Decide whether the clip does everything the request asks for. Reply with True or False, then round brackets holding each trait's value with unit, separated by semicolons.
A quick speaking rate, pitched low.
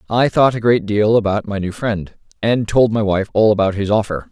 True (235 wpm; 105 Hz)